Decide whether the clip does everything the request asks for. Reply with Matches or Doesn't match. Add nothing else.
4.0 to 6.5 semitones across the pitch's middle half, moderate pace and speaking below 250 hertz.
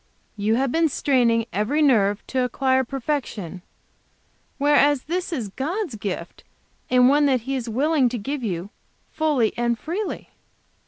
Doesn't match